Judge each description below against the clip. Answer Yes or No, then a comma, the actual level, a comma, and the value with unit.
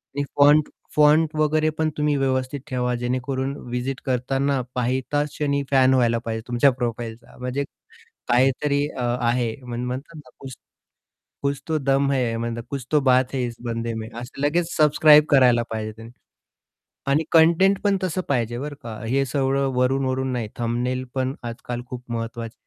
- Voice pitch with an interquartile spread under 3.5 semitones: Yes, average, 2.8 semitones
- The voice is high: No, low, 130 Hz